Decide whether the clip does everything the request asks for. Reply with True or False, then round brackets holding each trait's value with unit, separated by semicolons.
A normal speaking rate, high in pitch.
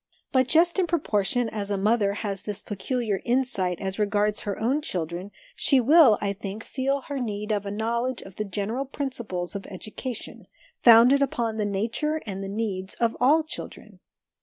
True (180 wpm; 220 Hz)